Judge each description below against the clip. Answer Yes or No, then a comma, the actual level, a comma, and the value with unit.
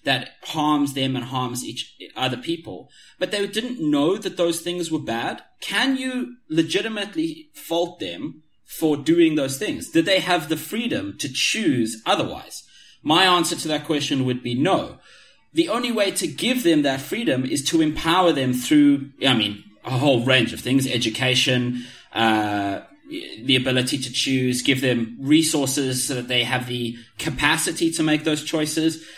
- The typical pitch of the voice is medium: Yes, medium, 150 Hz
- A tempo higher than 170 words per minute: No, average, 165 wpm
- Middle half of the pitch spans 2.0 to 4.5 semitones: No, wide, 5.6 semitones